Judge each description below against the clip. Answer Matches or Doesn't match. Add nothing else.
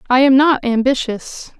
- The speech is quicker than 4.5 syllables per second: Doesn't match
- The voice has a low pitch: Doesn't match